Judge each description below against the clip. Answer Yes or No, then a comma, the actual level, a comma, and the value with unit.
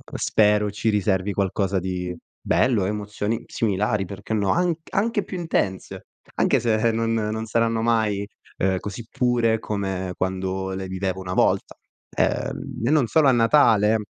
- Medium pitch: No, low, 105 Hz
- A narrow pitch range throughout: No, average, 3.1 semitones